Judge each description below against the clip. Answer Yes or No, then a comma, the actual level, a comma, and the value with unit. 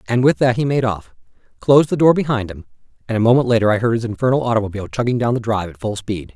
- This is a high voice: No, low, 115 Hz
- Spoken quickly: Yes, fast, 255 wpm